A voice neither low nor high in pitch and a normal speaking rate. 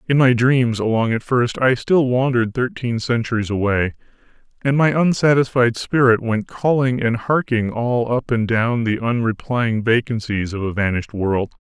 No: low, 120 Hz; average, 160 wpm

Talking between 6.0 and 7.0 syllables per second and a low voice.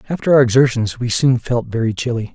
Yes: 6.1 syllables/s; low, 120 Hz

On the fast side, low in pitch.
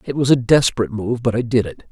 Yes: fast, 280 wpm; low, 115 Hz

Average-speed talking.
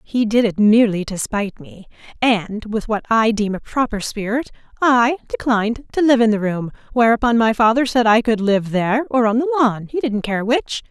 No: fast, 210 wpm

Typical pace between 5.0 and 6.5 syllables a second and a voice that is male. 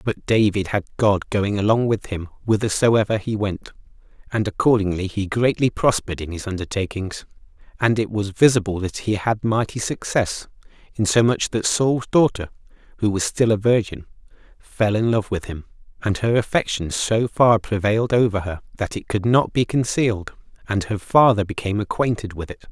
Yes: 5.1 syllables/s; male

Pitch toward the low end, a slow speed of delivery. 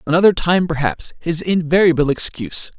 No: medium, 160 Hz; slow, 110 wpm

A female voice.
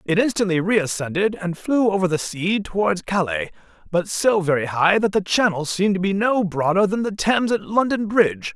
No: male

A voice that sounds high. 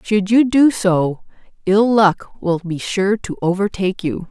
Yes: high, 200 Hz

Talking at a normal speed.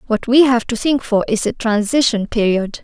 No: fast, 210 wpm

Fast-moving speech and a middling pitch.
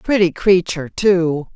No: slow, 115 wpm; medium, 180 Hz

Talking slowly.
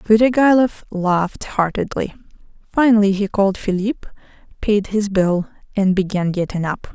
Yes: slow, 120 wpm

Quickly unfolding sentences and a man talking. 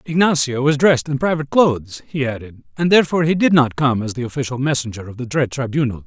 Yes: fast, 220 wpm; male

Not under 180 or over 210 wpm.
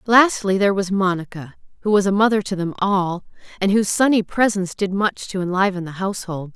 Yes: average, 190 wpm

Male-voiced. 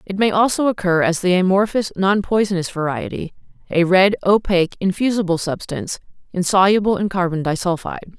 No: female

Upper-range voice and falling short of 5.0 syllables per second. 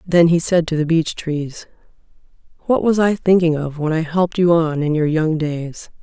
No: medium, 165 Hz; 4.7 syllables/s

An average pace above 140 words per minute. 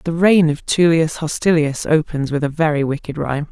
Yes: average, 190 wpm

